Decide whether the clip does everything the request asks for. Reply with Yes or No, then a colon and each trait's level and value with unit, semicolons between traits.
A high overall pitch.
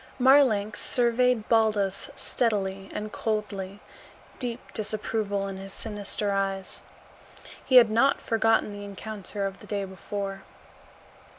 Yes: high, 210 Hz